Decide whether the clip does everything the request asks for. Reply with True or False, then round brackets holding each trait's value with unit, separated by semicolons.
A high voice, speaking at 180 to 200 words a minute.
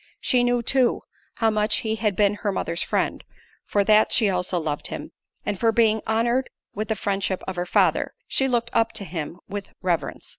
True (210 Hz; 195 wpm)